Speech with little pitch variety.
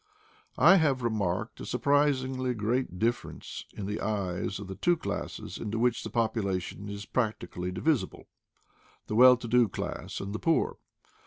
No: average, 4.2 semitones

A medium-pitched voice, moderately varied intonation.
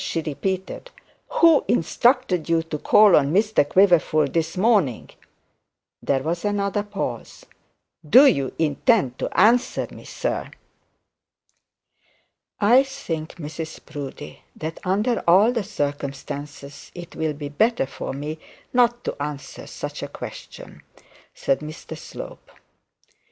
No: medium, 170 Hz; wide, 6.4 semitones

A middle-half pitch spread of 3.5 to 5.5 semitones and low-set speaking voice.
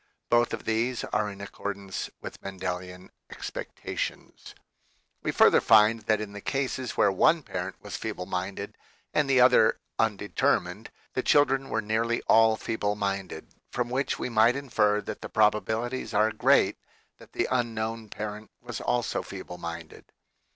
No: average, 3.1 semitones; low, 110 Hz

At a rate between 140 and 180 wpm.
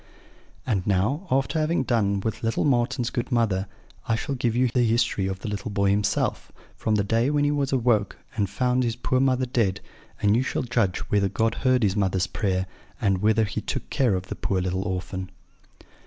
No: average, 200 wpm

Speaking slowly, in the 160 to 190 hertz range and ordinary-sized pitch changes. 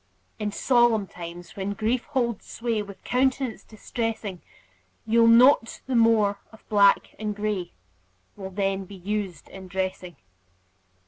No: slow, 130 wpm; high, 210 Hz; average, 3.0 semitones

